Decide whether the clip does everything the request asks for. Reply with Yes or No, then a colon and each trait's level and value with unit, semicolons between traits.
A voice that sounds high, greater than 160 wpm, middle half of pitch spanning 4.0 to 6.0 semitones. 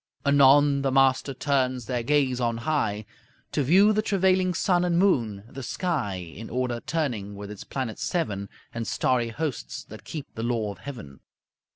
No: low, 130 Hz; average, 170 wpm; average, 5.0 semitones